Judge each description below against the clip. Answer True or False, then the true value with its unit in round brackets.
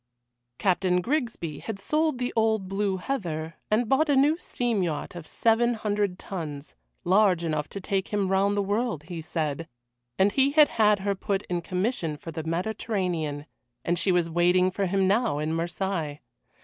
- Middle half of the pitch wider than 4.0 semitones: True (4.6 semitones)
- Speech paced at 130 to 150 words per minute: False (175 wpm)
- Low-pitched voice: False (190 Hz)